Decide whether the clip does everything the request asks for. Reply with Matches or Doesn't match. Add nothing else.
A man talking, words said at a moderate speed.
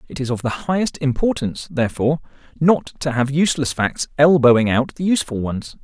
Matches